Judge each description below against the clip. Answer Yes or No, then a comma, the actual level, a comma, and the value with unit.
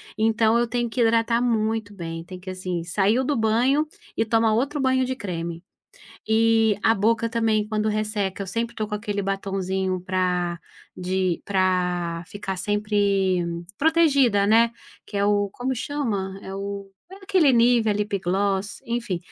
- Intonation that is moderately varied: Yes, average, 3.3 semitones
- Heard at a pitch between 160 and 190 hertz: No, high, 210 Hz